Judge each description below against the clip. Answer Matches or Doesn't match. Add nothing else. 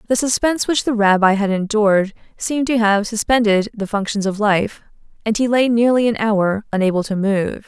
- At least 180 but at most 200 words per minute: Matches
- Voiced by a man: Doesn't match